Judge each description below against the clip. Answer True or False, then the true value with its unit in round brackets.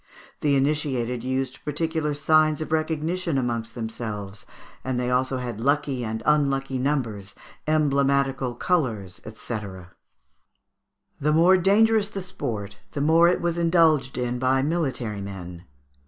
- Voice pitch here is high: False (135 Hz)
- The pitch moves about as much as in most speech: True (4.6 semitones)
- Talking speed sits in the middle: False (125 wpm)